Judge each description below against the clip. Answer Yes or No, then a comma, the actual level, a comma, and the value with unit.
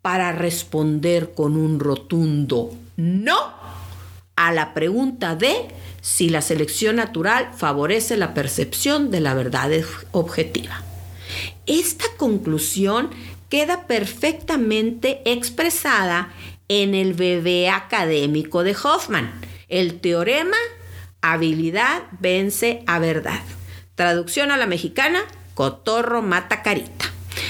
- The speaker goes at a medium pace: No, slow, 100 wpm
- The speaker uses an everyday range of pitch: No, wide, 8.2 semitones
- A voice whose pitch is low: No, medium, 170 Hz